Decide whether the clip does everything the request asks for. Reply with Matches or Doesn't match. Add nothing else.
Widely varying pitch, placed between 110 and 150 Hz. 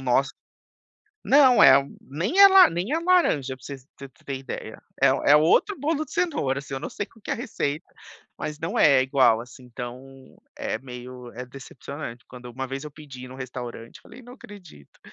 Matches